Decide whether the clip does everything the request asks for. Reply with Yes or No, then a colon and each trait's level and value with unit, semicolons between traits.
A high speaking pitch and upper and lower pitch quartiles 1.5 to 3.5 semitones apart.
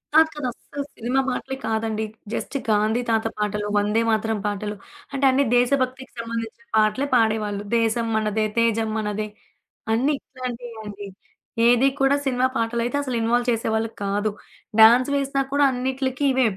Yes: high, 230 Hz; average, 3.0 semitones